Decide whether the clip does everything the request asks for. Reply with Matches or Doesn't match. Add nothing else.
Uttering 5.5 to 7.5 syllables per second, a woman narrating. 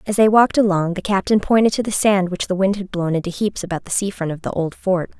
Matches